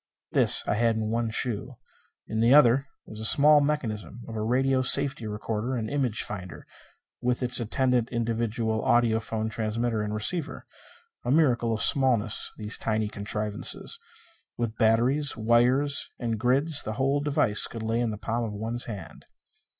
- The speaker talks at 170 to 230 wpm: No, average, 160 wpm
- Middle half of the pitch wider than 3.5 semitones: No, average, 2.9 semitones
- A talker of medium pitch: No, low, 115 Hz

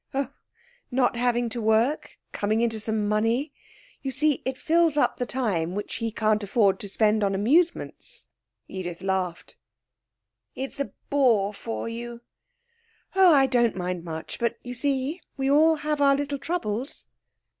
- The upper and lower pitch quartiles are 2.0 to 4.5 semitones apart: No, average, 4.9 semitones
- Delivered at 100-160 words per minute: Yes, average, 155 wpm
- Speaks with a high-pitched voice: Yes, high, 235 Hz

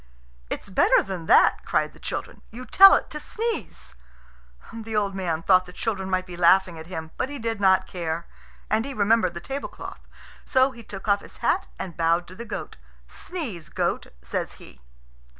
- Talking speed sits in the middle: Yes, average, 185 wpm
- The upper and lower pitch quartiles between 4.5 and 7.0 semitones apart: Yes, average, 4.8 semitones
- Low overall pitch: No, high, 190 Hz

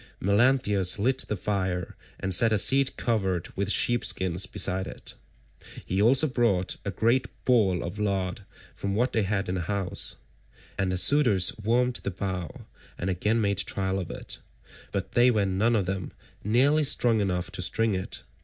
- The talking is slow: No, average, 175 wpm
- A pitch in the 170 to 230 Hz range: No, low, 100 Hz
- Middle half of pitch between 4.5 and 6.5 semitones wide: No, average, 3.8 semitones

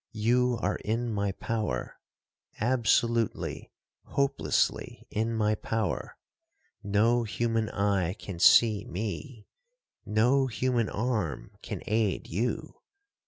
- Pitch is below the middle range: Yes, low, 115 Hz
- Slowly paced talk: Yes, slow, 90 wpm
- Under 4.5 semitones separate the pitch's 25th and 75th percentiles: Yes, average, 2.8 semitones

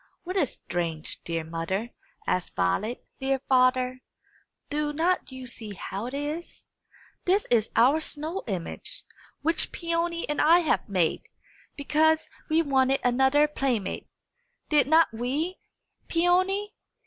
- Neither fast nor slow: No, slow, 125 wpm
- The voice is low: No, very high, 275 Hz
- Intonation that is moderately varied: No, wide, 5.7 semitones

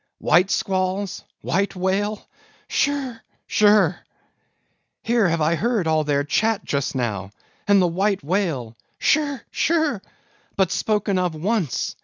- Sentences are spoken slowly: Yes, slow, 115 wpm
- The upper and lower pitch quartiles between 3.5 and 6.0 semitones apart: Yes, average, 4.8 semitones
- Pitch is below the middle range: No, high, 190 Hz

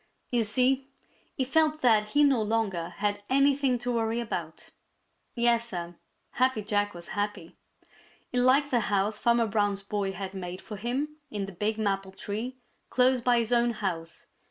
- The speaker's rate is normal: Yes, average, 165 wpm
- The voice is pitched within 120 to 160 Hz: No, high, 225 Hz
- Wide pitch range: No, average, 3.7 semitones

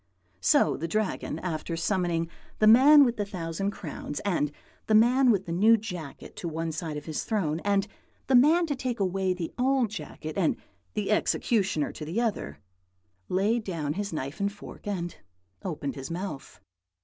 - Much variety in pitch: No, average, 4.9 semitones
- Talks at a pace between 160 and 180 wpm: Yes, average, 175 wpm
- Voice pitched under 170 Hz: No, high, 190 Hz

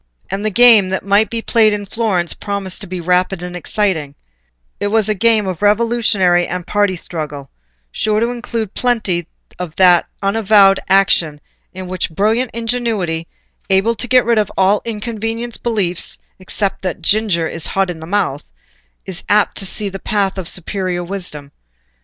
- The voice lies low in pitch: No, high, 195 Hz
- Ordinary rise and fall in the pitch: Yes, average, 3.5 semitones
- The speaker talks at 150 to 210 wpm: Yes, average, 165 wpm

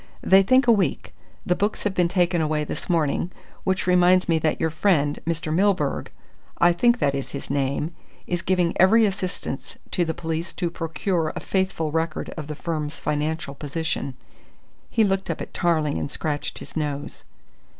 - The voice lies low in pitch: No, medium, 165 Hz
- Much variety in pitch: No, average, 3.5 semitones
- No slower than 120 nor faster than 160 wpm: No, average, 175 wpm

